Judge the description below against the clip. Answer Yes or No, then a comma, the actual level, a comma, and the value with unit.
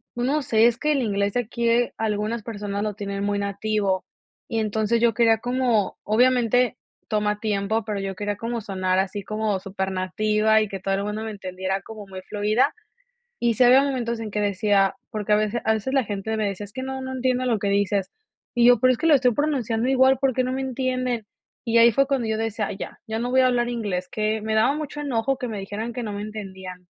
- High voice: Yes, high, 220 Hz